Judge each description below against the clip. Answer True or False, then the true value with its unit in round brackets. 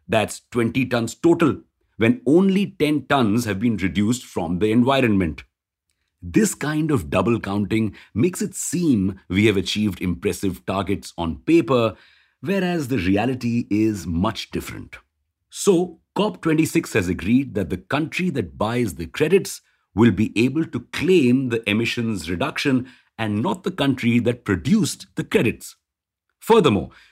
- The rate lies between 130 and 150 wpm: True (140 wpm)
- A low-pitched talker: True (115 Hz)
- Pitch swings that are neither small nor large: False (6.2 semitones)